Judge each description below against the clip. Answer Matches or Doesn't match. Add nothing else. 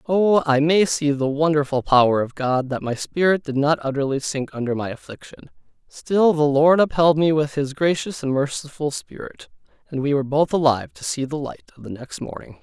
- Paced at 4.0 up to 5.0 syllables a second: Doesn't match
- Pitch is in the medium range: Matches